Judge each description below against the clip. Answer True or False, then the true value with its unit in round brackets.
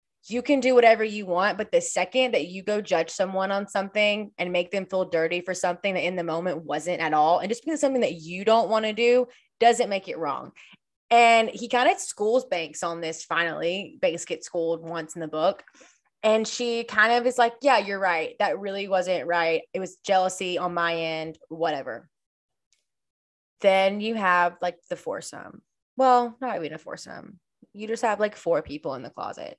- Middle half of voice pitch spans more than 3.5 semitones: True (5.0 semitones)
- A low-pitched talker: False (195 Hz)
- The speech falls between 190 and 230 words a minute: True (205 wpm)